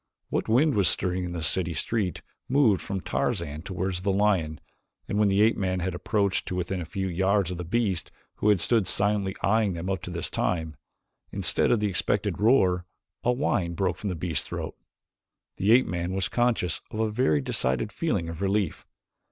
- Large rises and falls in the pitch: No, average, 3.2 semitones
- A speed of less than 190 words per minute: No, average, 195 wpm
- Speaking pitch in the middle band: No, very low, 95 Hz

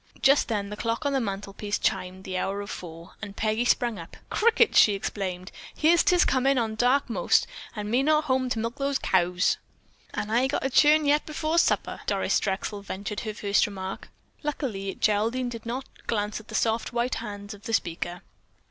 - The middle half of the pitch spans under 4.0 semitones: No, average, 4.8 semitones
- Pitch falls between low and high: No, high, 220 Hz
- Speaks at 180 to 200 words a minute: Yes, average, 190 wpm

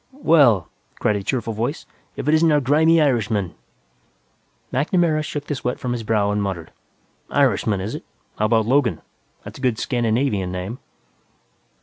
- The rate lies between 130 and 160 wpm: Yes, average, 155 wpm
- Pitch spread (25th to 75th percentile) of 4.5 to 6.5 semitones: Yes, wide, 5.6 semitones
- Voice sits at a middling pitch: No, low, 120 Hz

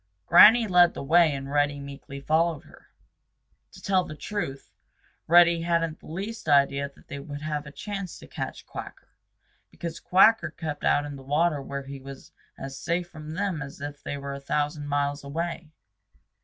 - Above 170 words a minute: Yes, average, 180 wpm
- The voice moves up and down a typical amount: Yes, average, 3.5 semitones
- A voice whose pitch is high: No, medium, 150 Hz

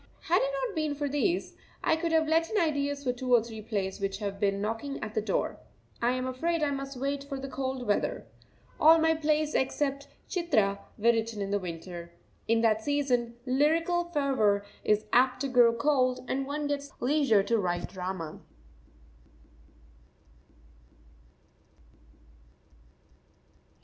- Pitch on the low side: No, very high, 260 Hz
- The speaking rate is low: No, average, 155 wpm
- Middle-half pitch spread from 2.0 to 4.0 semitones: No, average, 5.2 semitones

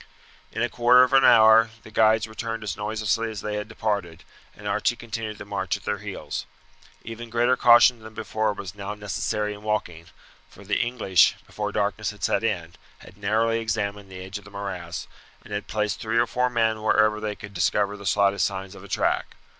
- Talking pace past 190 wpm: Yes, average, 200 wpm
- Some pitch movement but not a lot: No, narrow, 1.9 semitones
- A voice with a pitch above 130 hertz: No, low, 105 Hz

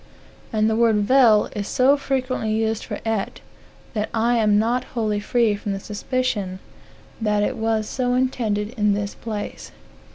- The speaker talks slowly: No, average, 155 wpm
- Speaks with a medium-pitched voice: No, high, 220 Hz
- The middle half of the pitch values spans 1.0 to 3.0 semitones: Yes, average, 2.7 semitones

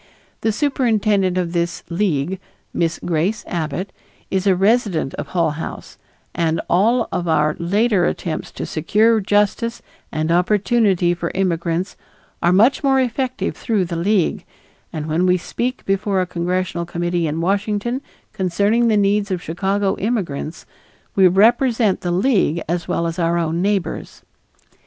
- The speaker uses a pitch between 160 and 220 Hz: Yes, medium, 185 Hz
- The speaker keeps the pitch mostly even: No, average, 3.7 semitones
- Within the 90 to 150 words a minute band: Yes, average, 145 wpm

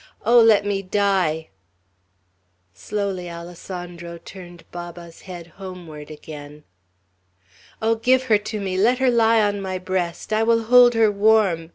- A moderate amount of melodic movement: Yes, average, 4.2 semitones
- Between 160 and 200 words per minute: No, average, 140 wpm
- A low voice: No, high, 190 Hz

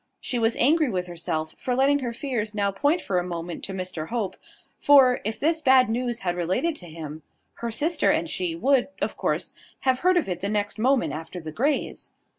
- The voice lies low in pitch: No, high, 220 Hz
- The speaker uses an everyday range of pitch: No, wide, 6.9 semitones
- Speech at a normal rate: No, fast, 210 wpm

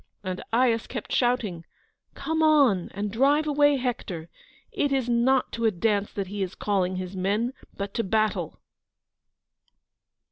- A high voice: Yes, high, 225 Hz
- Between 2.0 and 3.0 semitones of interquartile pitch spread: No, average, 4.9 semitones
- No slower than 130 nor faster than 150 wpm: Yes, average, 145 wpm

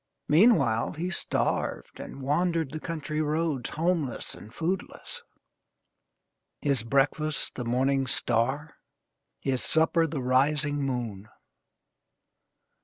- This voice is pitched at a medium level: Yes, medium, 145 Hz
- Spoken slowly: Yes, slow, 100 wpm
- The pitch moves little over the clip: No, average, 3.8 semitones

